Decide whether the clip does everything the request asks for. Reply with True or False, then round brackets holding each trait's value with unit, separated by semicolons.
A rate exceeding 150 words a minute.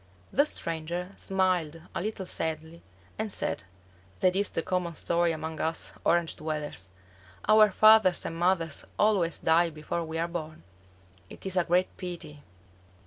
False (145 wpm)